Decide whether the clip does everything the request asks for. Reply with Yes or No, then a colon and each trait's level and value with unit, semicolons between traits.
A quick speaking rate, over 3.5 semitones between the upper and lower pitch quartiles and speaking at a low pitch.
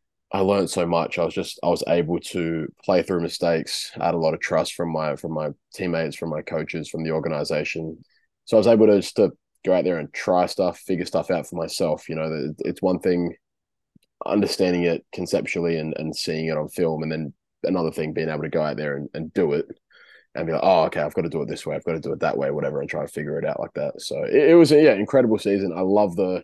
Yes: fast, 265 wpm; average, 4.5 semitones; very low, 85 Hz